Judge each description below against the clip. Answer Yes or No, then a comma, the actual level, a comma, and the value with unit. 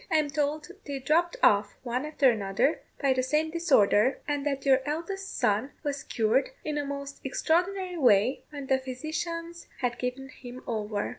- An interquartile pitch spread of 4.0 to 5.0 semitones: No, average, 3.6 semitones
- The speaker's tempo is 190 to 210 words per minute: No, average, 170 wpm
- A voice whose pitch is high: Yes, very high, 280 Hz